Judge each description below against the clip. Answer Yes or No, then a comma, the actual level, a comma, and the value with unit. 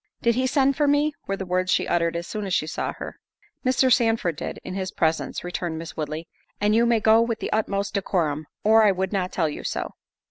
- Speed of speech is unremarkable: No, fast, 235 wpm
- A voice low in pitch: No, high, 195 Hz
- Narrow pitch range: No, average, 5.0 semitones